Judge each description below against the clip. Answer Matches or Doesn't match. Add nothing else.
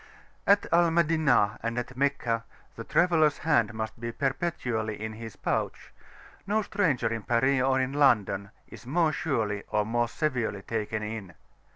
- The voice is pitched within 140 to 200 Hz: Doesn't match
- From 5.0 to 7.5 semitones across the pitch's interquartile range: Matches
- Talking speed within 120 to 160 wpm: Matches